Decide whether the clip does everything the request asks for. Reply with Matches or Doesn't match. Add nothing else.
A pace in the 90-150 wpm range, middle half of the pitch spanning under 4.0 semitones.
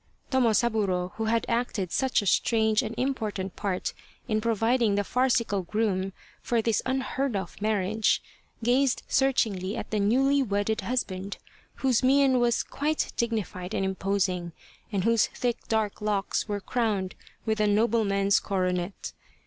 Matches